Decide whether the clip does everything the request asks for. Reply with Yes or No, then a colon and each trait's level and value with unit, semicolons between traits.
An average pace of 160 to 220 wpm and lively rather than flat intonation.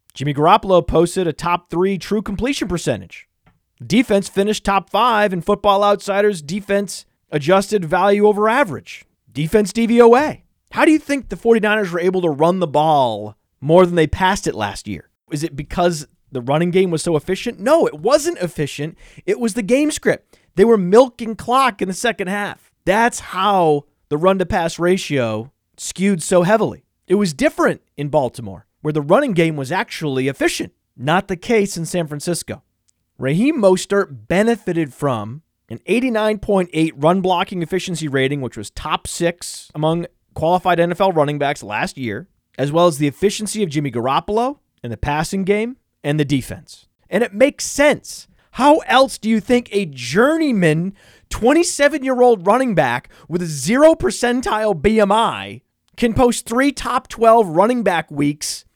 Yes: average, 165 wpm; wide, 6.4 semitones